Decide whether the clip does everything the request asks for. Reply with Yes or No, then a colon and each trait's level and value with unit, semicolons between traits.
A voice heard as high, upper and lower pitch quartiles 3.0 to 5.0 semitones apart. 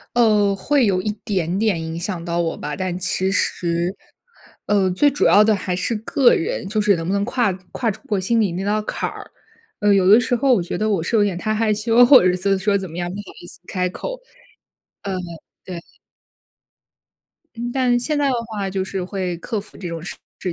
Yes: high, 200 Hz; average, 3.4 semitones